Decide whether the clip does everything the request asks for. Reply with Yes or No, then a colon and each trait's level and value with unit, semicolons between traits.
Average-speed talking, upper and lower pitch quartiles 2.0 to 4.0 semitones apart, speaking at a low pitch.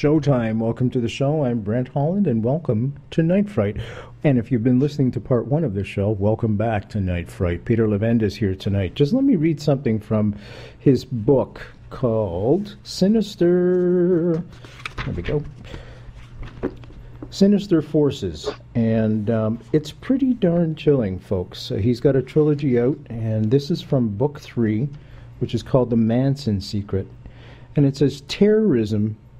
No: average, 160 wpm; average, 4.8 semitones; low, 125 Hz